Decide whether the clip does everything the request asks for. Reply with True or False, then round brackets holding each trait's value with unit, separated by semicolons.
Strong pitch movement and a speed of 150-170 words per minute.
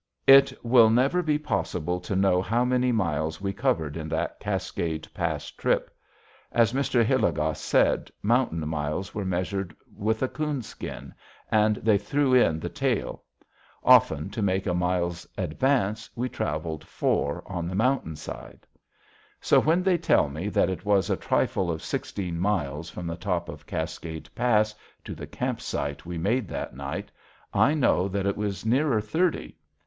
True (6.2 semitones; 165 wpm)